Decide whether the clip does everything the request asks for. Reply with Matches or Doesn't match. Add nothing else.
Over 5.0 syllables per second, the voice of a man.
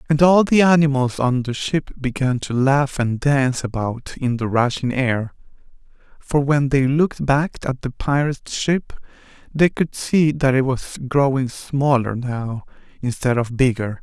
Doesn't match